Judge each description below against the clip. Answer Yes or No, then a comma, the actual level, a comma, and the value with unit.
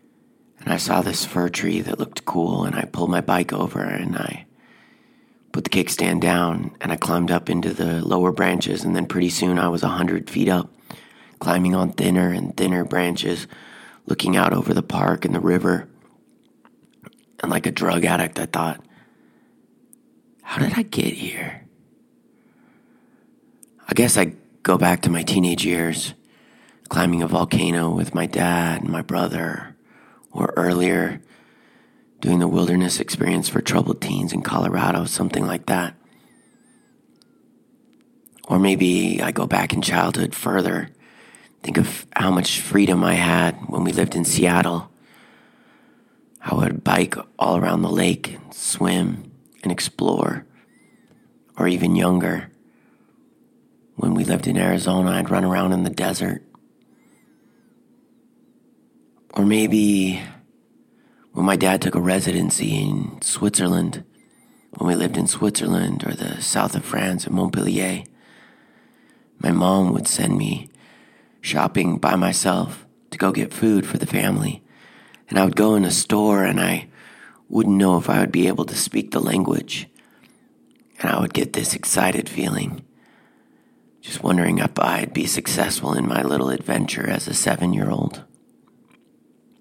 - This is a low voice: Yes, very low, 90 Hz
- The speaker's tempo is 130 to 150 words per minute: Yes, average, 145 wpm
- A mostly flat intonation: Yes, narrow, 2.2 semitones